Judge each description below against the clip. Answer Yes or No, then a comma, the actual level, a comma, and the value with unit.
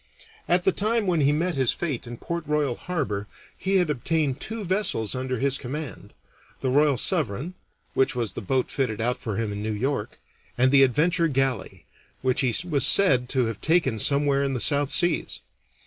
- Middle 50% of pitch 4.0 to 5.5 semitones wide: Yes, average, 4.8 semitones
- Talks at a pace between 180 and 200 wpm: Yes, average, 190 wpm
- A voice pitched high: No, low, 135 Hz